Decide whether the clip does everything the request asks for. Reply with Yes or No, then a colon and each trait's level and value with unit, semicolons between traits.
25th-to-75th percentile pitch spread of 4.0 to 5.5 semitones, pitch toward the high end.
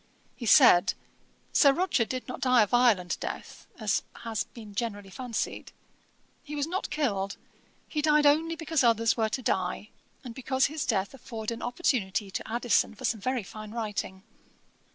Yes: average, 4.6 semitones; high, 235 Hz